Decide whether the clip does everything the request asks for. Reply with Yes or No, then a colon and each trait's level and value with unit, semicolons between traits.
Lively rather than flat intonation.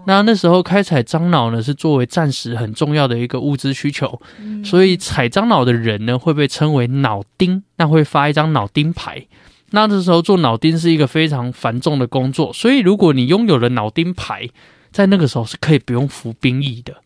Yes: wide, 5.7 semitones